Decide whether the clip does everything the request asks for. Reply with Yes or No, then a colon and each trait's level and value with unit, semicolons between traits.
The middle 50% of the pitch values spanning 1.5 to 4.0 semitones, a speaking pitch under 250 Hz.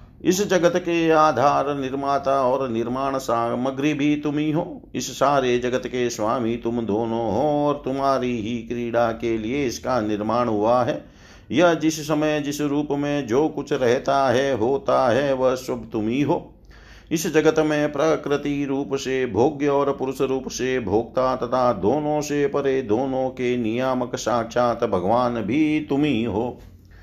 Yes: average, 3.4 semitones; low, 135 Hz